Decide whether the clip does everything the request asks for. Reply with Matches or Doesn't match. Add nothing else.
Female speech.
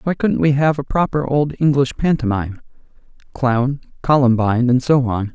Doesn't match